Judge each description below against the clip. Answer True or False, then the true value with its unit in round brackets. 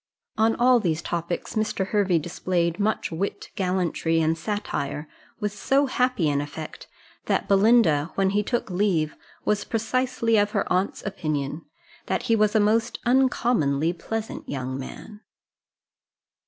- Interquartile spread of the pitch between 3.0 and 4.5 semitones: False (5.3 semitones)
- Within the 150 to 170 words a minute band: False (140 wpm)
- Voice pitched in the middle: False (195 Hz)